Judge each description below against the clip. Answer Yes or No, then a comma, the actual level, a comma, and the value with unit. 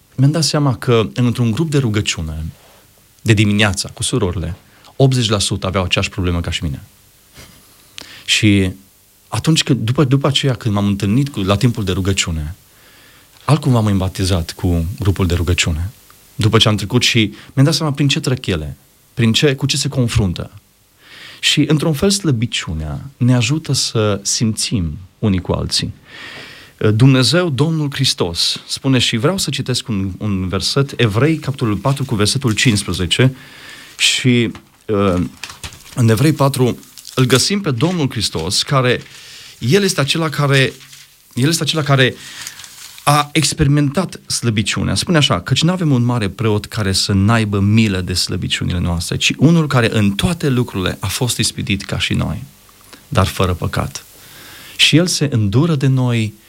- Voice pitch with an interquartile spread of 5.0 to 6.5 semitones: Yes, wide, 5.6 semitones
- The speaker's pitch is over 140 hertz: No, low, 115 Hz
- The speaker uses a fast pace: No, average, 150 wpm